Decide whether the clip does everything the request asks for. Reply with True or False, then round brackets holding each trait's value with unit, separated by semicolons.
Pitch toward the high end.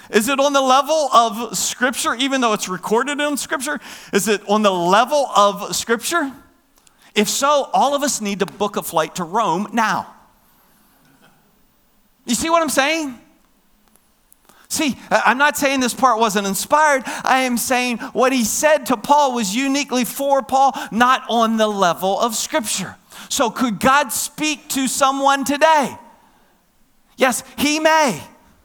True (255 Hz)